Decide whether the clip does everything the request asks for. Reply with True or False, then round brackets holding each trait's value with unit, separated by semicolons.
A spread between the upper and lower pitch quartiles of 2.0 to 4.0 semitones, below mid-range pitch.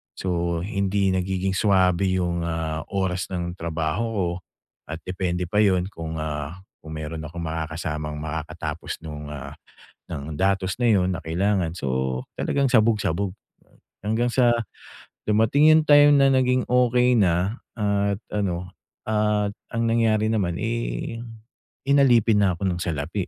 False (4.8 semitones; 95 Hz)